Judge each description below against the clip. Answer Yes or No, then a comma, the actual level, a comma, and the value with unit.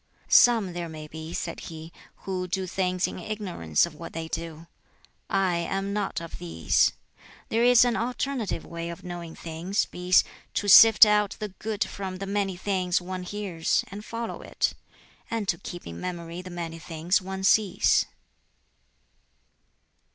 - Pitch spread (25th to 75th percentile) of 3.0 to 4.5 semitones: Yes, average, 3.3 semitones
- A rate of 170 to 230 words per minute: No, average, 160 wpm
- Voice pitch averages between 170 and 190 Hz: Yes, medium, 185 Hz